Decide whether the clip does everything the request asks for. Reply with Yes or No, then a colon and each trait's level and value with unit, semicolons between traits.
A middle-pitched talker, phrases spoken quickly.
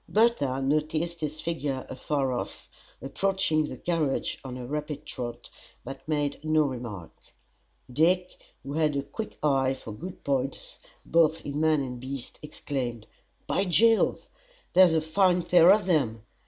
No: medium, 150 Hz; average, 145 wpm